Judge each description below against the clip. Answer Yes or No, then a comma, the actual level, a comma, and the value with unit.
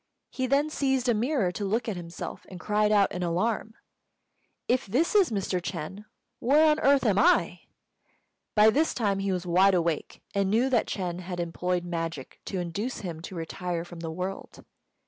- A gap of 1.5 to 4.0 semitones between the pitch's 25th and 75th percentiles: No, average, 5.0 semitones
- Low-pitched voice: No, high, 195 Hz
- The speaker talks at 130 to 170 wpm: No, average, 185 wpm